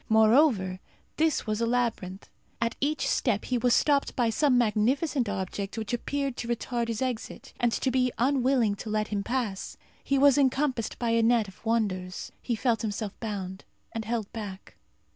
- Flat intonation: No, average, 3.3 semitones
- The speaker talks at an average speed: Yes, average, 175 wpm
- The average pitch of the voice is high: Yes, high, 230 Hz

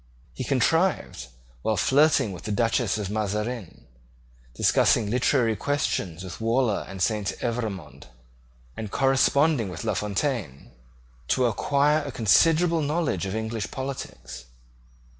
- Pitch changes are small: No, wide, 5.6 semitones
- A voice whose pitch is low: Yes, low, 115 Hz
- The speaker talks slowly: Yes, slow, 120 wpm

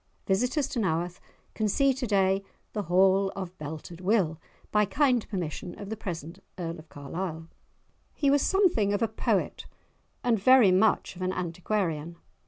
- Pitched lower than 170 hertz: No, high, 190 Hz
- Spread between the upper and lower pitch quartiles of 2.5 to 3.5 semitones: No, average, 4.3 semitones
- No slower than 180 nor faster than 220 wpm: No, average, 160 wpm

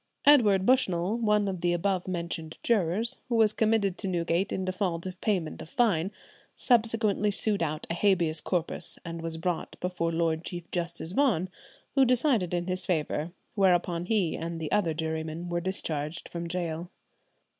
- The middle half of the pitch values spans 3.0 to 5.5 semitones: Yes, average, 3.6 semitones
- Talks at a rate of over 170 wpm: No, average, 165 wpm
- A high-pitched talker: No, medium, 180 Hz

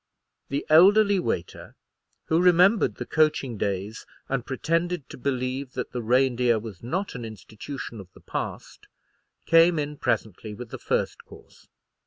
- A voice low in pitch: Yes, low, 130 Hz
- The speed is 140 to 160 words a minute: Yes, average, 145 wpm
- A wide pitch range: Yes, wide, 6.3 semitones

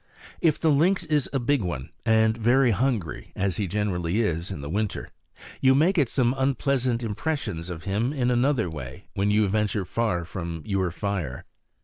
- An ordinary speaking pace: Yes, average, 170 wpm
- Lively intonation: Yes, wide, 6.3 semitones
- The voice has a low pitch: Yes, low, 110 Hz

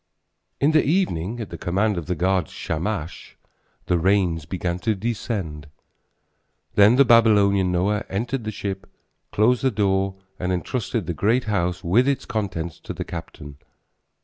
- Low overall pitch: Yes, low, 100 Hz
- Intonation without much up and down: No, average, 4.3 semitones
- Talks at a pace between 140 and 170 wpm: Yes, average, 155 wpm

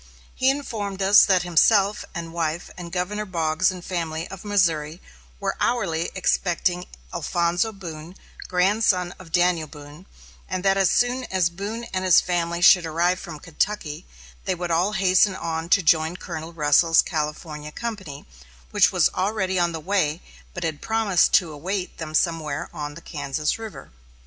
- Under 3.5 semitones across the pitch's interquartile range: Yes, average, 3.1 semitones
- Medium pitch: Yes, medium, 175 Hz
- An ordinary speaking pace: Yes, average, 160 wpm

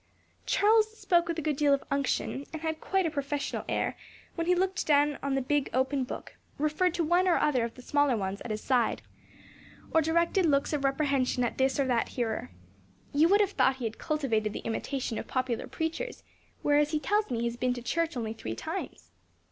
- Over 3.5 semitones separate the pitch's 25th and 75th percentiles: Yes, average, 4.5 semitones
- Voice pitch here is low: No, very high, 285 Hz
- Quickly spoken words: Yes, fast, 210 wpm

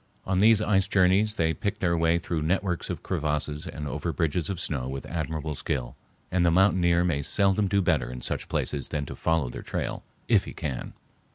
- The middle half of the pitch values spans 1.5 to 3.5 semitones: No, average, 4.1 semitones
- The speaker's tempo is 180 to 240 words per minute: Yes, average, 200 wpm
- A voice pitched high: No, very low, 85 Hz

